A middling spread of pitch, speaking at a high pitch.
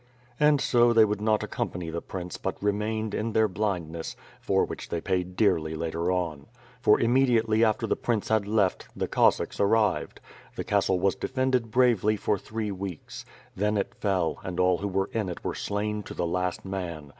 No: average, 3.4 semitones; low, 100 Hz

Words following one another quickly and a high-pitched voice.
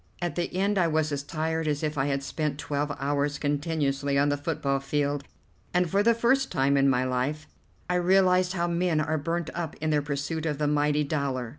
No: fast, 210 wpm; medium, 150 Hz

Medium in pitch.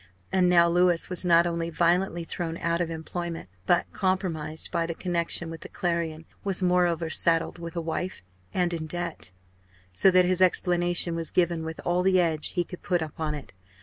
Yes: medium, 170 Hz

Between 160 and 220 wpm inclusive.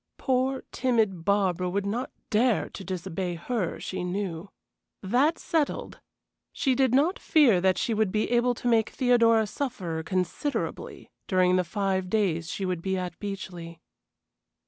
No: average, 145 wpm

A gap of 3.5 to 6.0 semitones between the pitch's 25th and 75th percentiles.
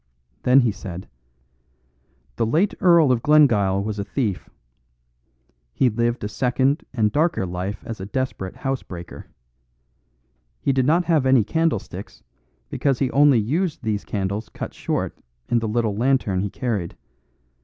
Yes: average, 5.0 semitones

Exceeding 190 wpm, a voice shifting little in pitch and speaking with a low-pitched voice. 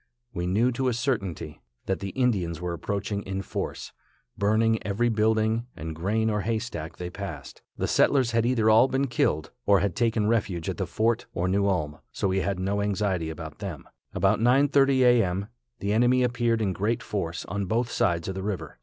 No: average, 200 wpm; average, 4.1 semitones; low, 100 Hz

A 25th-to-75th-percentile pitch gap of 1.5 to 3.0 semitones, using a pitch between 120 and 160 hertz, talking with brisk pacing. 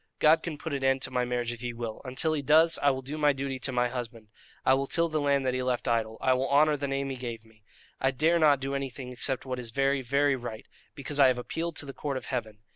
Yes: narrow, 2.6 semitones; low, 135 Hz; fast, 275 wpm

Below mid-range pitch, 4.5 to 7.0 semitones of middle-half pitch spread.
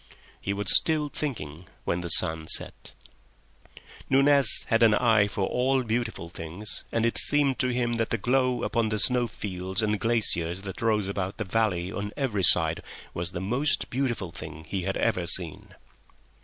Yes: low, 105 Hz; average, 4.9 semitones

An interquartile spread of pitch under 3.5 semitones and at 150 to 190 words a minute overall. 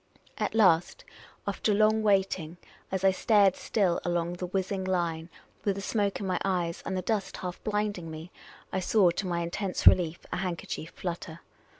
Yes: narrow, 2.6 semitones; average, 185 wpm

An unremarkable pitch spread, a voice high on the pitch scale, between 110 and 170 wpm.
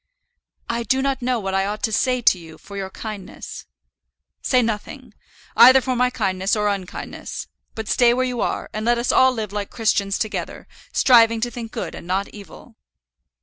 No: average, 3.8 semitones; high, 225 Hz; average, 185 wpm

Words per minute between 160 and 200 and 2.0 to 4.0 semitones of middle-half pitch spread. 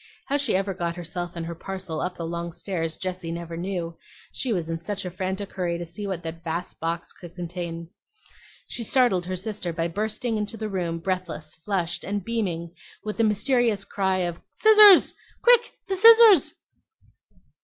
Yes: average, 175 wpm; average, 3.7 semitones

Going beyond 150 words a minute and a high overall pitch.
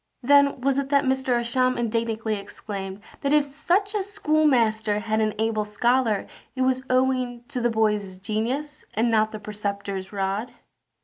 Yes: average, 160 wpm; high, 235 Hz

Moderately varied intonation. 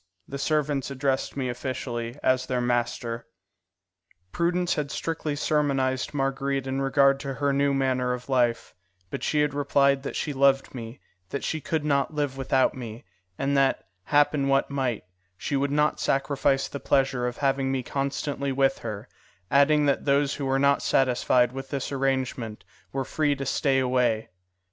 No: narrow, 1.5 semitones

